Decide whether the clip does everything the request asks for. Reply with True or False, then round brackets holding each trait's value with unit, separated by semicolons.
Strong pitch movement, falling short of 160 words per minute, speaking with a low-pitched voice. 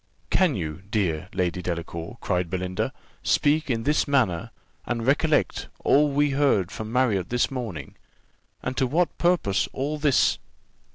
True (7.9 semitones; 145 wpm; 120 Hz)